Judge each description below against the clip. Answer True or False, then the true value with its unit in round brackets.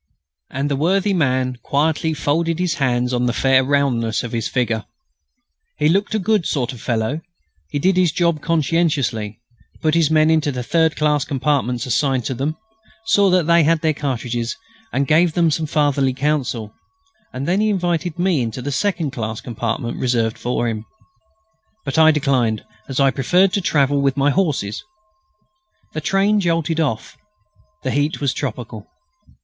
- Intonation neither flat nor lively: True (4.7 semitones)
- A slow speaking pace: False (165 wpm)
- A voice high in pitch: False (145 Hz)